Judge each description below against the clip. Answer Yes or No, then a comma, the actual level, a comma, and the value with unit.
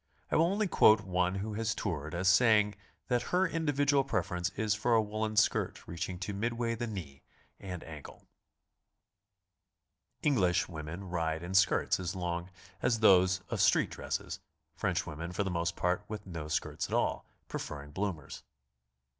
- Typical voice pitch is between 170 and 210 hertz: No, very low, 95 Hz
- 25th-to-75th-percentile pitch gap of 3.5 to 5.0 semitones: Yes, average, 4.2 semitones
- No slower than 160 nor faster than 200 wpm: Yes, average, 165 wpm